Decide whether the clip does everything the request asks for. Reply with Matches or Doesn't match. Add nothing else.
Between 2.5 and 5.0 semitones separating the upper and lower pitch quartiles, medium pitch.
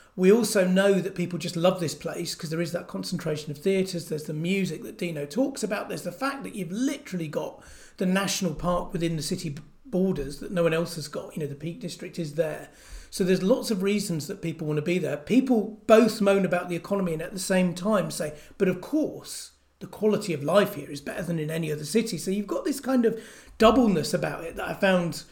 Matches